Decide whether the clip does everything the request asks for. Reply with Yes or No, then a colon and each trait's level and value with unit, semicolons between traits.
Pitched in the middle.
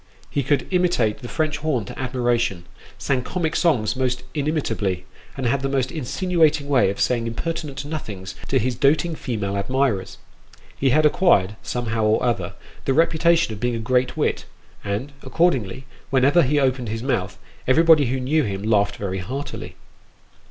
No: low, 130 Hz